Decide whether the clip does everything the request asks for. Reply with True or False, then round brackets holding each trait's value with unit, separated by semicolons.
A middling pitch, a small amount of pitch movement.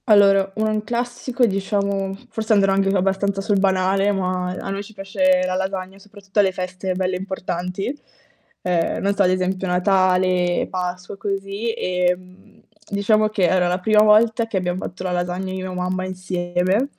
False (195 Hz; 1.7 semitones)